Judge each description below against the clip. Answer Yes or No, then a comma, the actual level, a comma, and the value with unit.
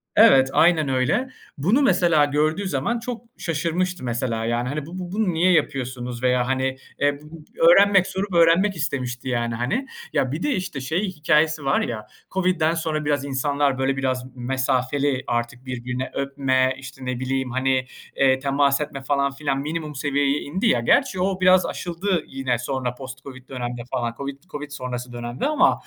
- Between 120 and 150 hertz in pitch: Yes, medium, 140 Hz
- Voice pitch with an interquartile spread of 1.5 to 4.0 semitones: No, average, 4.4 semitones